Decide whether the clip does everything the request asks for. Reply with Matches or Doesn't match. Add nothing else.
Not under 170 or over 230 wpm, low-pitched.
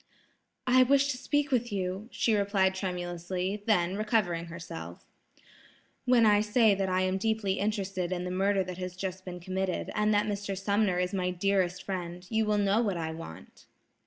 Doesn't match